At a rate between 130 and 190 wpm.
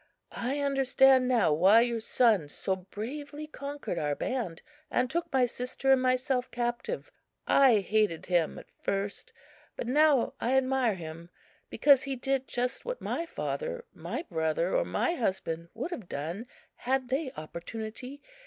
Yes: average, 150 wpm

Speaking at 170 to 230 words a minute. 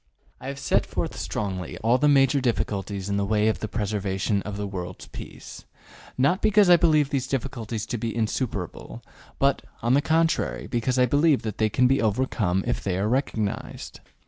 Yes: average, 185 wpm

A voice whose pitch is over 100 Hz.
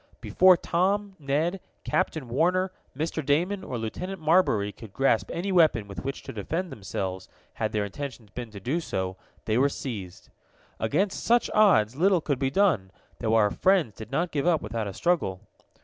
Yes: medium, 140 Hz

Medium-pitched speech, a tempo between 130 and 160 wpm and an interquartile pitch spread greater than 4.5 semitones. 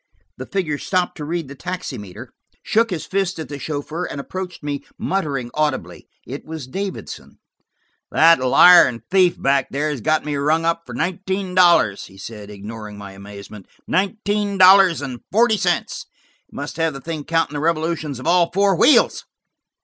No: medium, 160 Hz; average, 170 wpm; average, 5.0 semitones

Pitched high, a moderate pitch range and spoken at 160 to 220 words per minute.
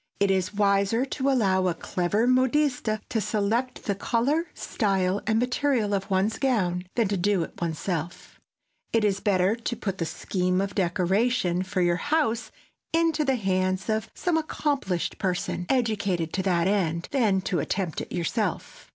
Yes: high, 200 Hz; average, 4.5 semitones; average, 165 wpm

